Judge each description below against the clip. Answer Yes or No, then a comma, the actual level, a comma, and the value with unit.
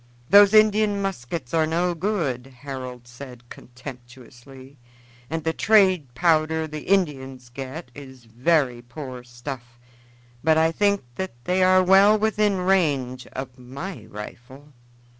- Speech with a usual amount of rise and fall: No, wide, 6.6 semitones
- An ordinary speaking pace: No, slow, 125 wpm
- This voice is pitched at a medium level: Yes, medium, 145 Hz